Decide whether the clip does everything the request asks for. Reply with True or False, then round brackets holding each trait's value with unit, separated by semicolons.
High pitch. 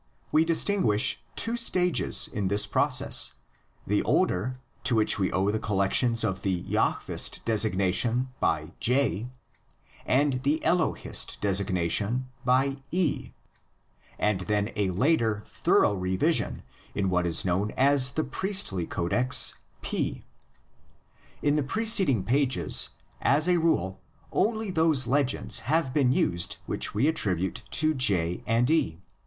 False (120 Hz)